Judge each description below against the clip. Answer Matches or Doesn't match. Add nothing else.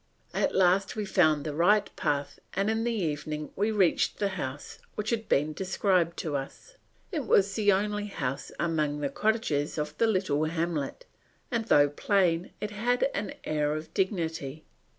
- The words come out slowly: Doesn't match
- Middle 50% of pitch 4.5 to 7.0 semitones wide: Matches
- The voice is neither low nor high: Matches